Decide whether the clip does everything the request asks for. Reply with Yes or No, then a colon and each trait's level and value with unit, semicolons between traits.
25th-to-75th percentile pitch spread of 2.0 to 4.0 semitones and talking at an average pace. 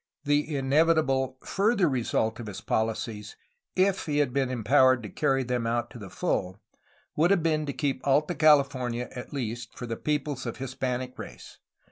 Yes: average, 3.7 semitones; average, 170 wpm